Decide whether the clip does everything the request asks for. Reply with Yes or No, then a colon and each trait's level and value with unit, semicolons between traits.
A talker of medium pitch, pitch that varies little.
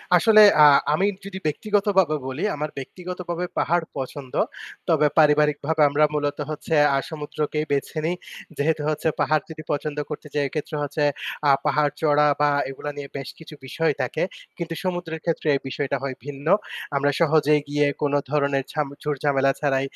Yes: medium, 150 Hz; narrow, 2.1 semitones